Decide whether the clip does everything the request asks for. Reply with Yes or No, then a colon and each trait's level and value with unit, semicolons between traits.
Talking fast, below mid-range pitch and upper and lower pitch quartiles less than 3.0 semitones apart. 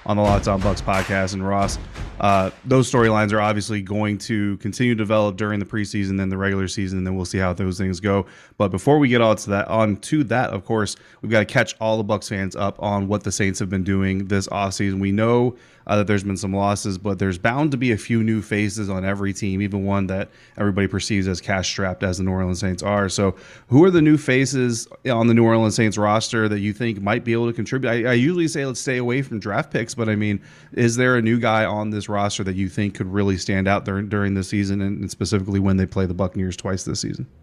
Yes: fast, 255 wpm; low, 105 Hz; narrow, 2.4 semitones